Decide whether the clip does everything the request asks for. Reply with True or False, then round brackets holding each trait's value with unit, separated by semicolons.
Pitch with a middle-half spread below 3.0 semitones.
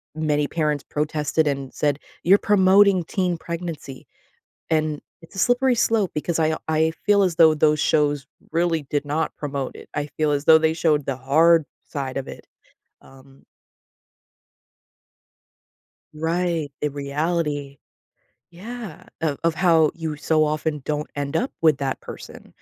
True (2.5 semitones)